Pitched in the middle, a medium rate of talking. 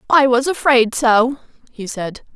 No: high, 245 Hz; average, 155 wpm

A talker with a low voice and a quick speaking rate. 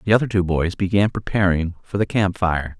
Yes: very low, 95 Hz; fast, 215 wpm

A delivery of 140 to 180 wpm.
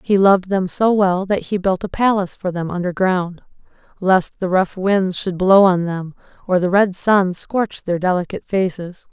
No: average, 190 wpm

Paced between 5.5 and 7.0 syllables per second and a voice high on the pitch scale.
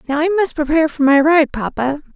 Yes: 5.9 syllables/s; very high, 300 Hz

